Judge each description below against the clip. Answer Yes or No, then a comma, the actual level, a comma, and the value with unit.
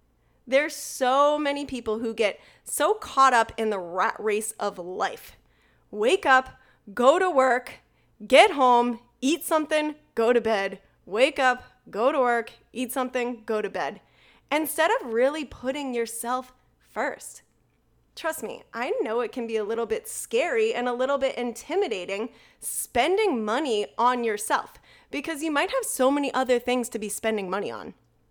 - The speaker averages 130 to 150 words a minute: No, average, 160 wpm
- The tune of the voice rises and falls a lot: No, average, 4.1 semitones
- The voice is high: Yes, very high, 255 Hz